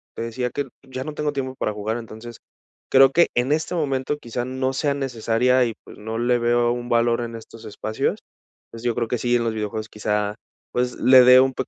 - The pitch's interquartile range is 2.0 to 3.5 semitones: Yes, narrow, 2.4 semitones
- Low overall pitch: Yes, low, 120 Hz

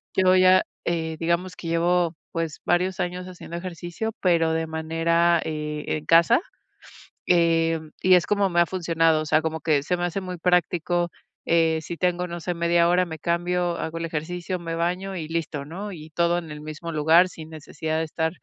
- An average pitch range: No, narrow, 1.7 semitones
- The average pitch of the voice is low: No, medium, 170 Hz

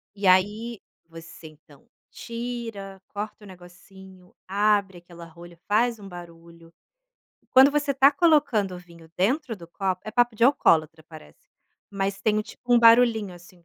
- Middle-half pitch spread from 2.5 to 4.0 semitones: No, average, 5.0 semitones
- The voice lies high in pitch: Yes, high, 195 Hz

